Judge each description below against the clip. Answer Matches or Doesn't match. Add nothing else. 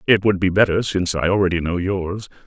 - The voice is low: Matches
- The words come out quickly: Matches